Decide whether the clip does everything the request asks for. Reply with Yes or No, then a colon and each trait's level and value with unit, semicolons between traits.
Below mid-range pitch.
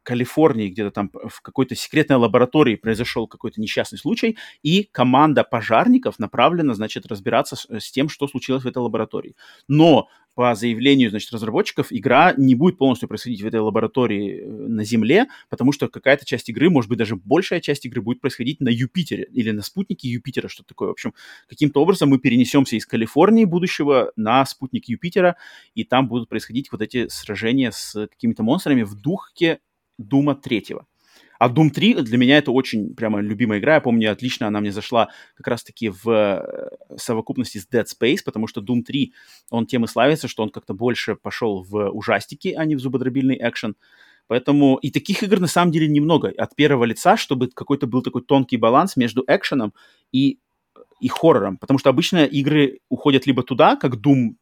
Yes: low, 130 Hz